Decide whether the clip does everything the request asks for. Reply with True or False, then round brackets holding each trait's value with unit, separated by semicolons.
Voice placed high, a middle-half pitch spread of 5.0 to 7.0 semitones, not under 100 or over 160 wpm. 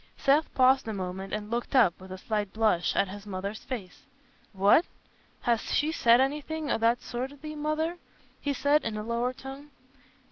False (235 Hz; 5.5 semitones; 185 wpm)